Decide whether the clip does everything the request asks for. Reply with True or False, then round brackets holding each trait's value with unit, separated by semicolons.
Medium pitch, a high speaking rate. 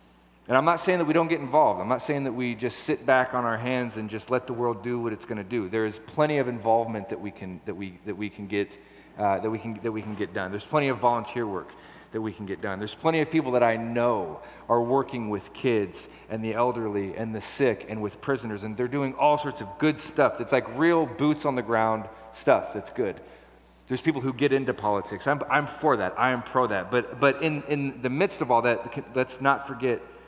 False (120 Hz; 230 wpm)